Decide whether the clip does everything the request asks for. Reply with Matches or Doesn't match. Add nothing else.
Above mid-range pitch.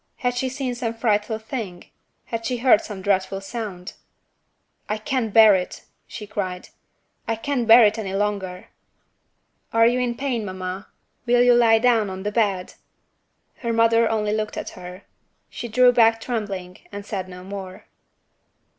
Matches